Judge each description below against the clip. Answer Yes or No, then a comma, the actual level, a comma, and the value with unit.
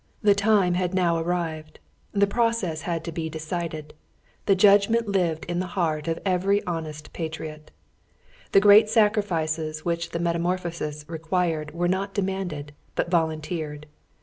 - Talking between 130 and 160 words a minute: Yes, slow, 135 wpm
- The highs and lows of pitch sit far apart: No, average, 3.5 semitones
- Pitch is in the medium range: Yes, medium, 170 Hz